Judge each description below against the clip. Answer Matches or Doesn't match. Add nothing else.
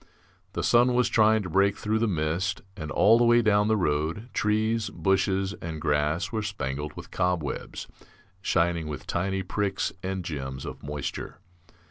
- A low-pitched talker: Matches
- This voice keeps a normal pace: Matches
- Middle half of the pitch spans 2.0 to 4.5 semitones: Doesn't match